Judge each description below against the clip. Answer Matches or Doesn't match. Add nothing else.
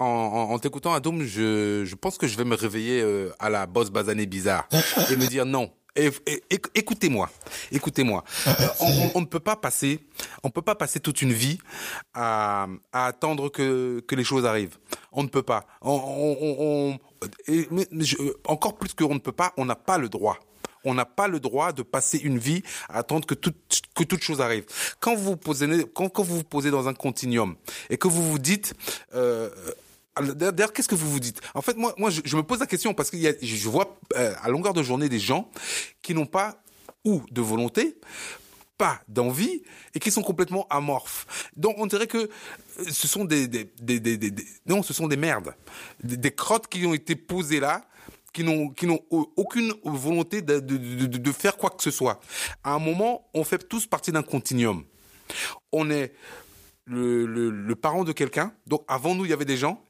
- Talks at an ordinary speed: Matches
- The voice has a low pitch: Doesn't match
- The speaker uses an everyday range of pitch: Doesn't match